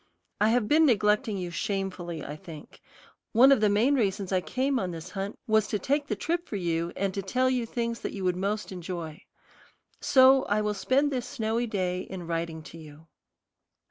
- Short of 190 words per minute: No, average, 200 wpm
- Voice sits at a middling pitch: No, high, 205 Hz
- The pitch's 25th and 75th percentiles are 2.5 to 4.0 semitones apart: No, average, 5.0 semitones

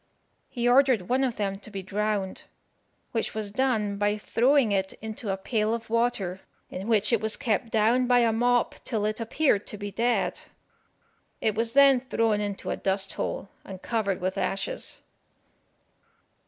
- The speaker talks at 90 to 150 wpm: No, average, 170 wpm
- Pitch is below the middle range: No, high, 220 Hz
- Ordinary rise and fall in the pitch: Yes, average, 3.1 semitones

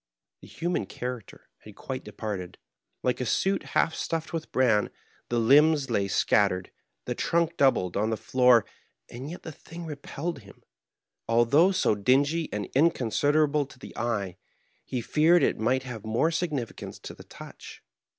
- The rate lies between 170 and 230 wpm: No, average, 160 wpm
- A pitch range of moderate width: No, wide, 6.1 semitones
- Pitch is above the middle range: No, low, 130 Hz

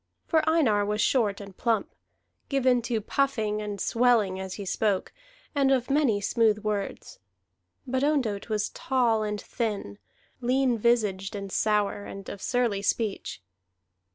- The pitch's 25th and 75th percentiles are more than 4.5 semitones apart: No, average, 3.5 semitones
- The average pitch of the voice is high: Yes, high, 215 Hz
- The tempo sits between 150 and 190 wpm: No, average, 140 wpm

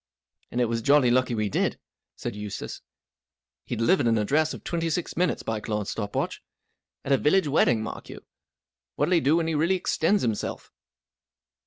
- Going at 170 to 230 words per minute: Yes, average, 175 wpm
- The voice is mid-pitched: No, low, 130 Hz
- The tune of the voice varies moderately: No, wide, 6.5 semitones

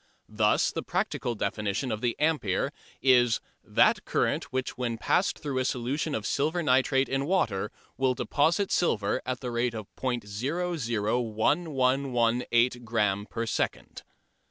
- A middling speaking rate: No, slow, 130 wpm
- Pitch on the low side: Yes, low, 125 Hz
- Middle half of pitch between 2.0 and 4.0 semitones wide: Yes, average, 3.4 semitones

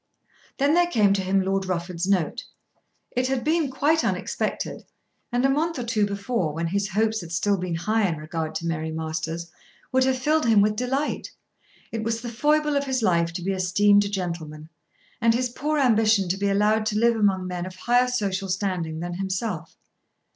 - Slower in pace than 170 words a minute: No, average, 195 wpm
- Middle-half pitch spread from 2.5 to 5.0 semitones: No, wide, 5.5 semitones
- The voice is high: Yes, high, 200 Hz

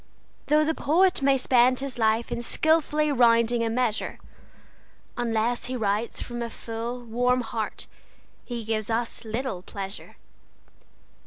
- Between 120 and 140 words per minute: Yes, slow, 135 wpm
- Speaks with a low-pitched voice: No, high, 240 Hz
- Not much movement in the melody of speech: Yes, narrow, 2.3 semitones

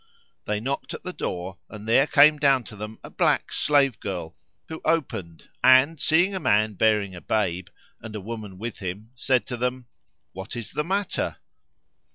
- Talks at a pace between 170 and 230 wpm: Yes, average, 180 wpm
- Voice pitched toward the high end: No, low, 115 Hz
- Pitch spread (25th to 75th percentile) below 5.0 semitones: No, wide, 5.4 semitones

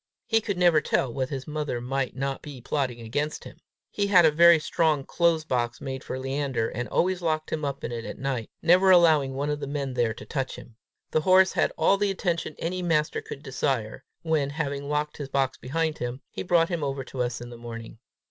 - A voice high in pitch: No, medium, 145 Hz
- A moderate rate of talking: No, fast, 225 wpm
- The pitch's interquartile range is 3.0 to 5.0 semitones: Yes, average, 3.9 semitones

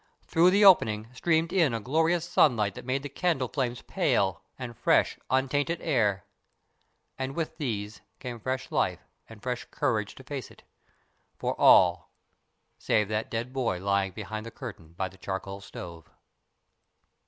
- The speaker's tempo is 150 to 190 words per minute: Yes, average, 155 wpm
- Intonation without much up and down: No, wide, 5.5 semitones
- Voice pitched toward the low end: Yes, low, 120 Hz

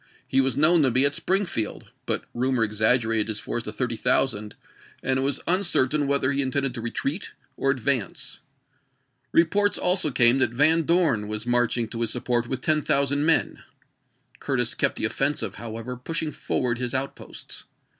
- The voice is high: No, low, 130 Hz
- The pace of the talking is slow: No, average, 175 wpm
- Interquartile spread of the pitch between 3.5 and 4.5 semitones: Yes, average, 3.8 semitones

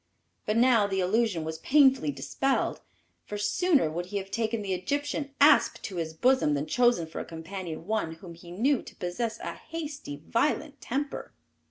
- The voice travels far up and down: Yes, wide, 7.6 semitones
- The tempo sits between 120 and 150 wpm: No, average, 175 wpm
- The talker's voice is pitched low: No, high, 210 Hz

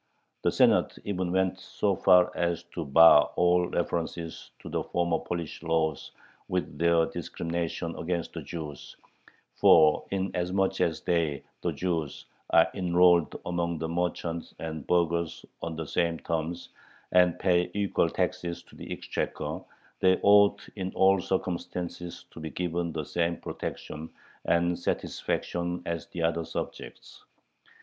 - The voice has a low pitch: Yes, very low, 85 Hz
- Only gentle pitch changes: Yes, narrow, 1.5 semitones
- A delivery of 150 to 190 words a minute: No, slow, 135 wpm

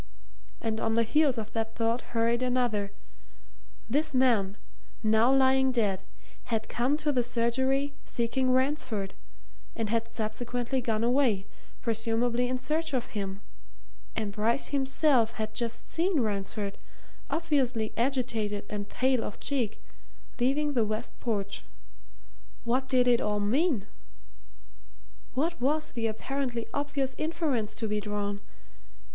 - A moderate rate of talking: No, slow, 130 wpm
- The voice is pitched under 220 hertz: No, high, 235 Hz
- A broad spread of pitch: No, average, 3.5 semitones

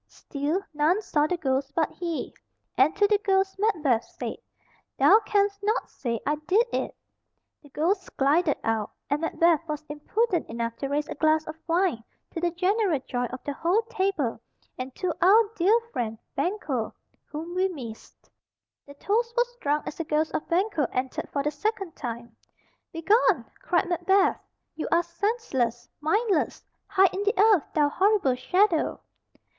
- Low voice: No, very high, 330 Hz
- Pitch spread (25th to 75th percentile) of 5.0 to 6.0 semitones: Yes, wide, 5.6 semitones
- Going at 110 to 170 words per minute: Yes, average, 160 wpm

